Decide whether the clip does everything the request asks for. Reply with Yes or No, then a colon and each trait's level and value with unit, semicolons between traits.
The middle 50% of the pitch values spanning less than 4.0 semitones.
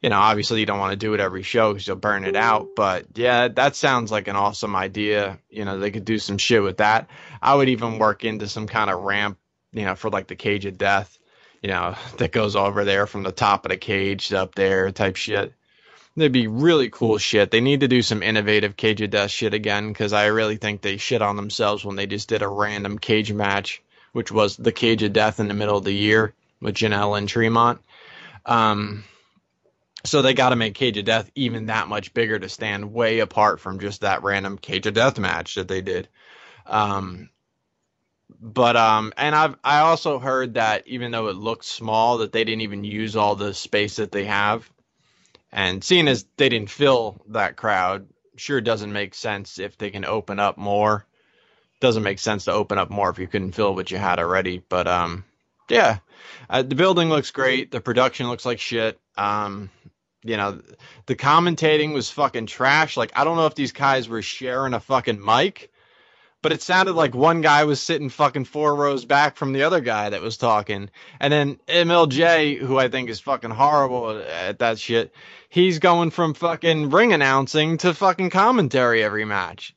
No: average, 4.7 semitones